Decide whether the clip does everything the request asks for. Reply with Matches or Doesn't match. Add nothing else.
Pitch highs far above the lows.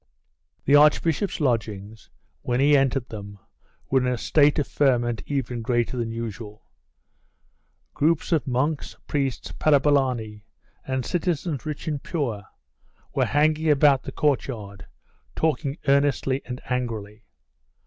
Doesn't match